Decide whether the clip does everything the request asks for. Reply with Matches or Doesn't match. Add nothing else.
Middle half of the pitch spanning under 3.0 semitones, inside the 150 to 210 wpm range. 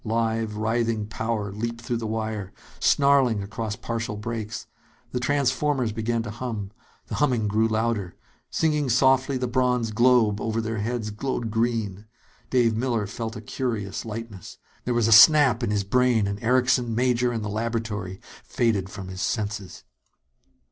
Matches